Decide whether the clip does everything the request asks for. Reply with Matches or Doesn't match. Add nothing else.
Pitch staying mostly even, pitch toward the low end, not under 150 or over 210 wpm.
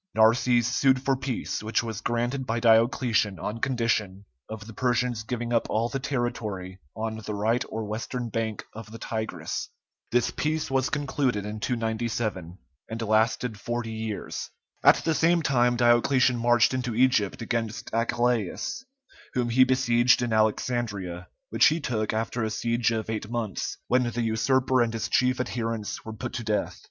Matches